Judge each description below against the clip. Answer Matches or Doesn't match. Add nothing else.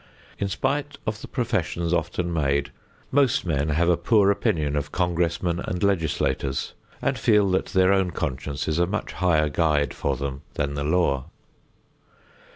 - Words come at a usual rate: Matches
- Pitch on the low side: Matches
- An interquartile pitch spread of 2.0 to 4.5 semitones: Doesn't match